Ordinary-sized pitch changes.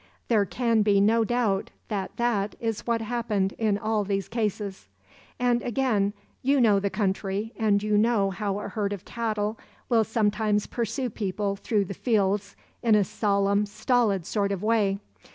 No: narrow, 2.3 semitones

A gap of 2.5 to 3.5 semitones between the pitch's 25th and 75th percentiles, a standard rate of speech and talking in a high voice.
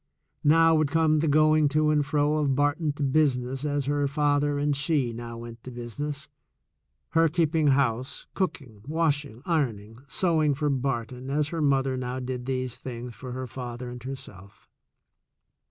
No: average, 3.2 semitones; average, 160 wpm; medium, 140 Hz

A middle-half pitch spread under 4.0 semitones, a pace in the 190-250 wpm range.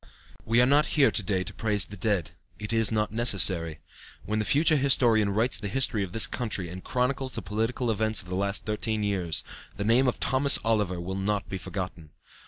Yes: average, 3.5 semitones; fast, 205 wpm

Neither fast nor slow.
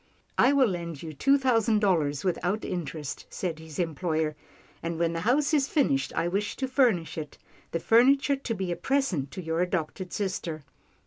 Yes: average, 195 wpm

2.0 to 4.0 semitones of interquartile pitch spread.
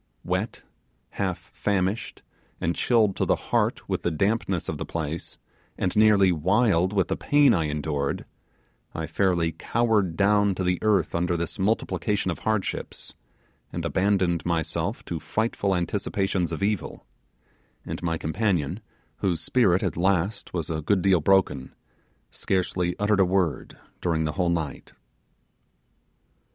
Yes: average, 3.3 semitones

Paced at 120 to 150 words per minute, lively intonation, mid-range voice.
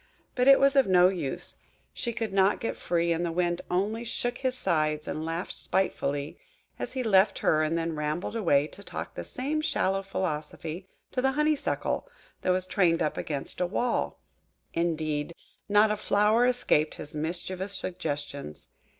No: average, 165 wpm; wide, 5.7 semitones; medium, 180 Hz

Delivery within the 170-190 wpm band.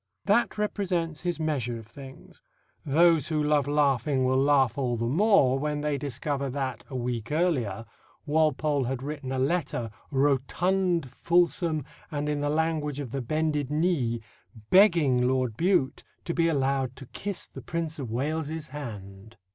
No: average, 155 wpm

